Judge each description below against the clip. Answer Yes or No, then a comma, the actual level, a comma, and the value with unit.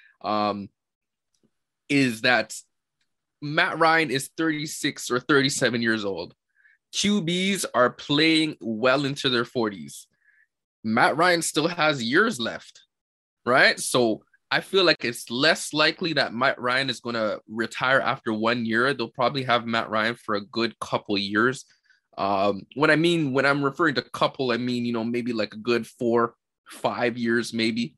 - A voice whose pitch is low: Yes, low, 125 Hz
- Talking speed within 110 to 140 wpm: No, average, 155 wpm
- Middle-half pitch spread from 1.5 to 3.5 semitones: No, average, 4.7 semitones